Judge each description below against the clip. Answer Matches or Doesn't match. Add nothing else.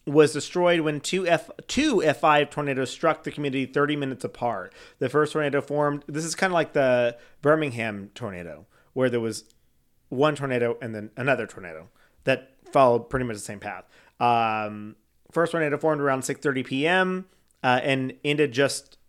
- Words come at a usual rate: Matches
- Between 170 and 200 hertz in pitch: Doesn't match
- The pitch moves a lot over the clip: Doesn't match